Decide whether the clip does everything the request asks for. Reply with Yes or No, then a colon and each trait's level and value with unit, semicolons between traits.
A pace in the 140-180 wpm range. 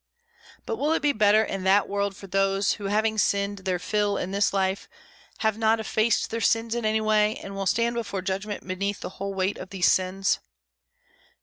No: average, 200 wpm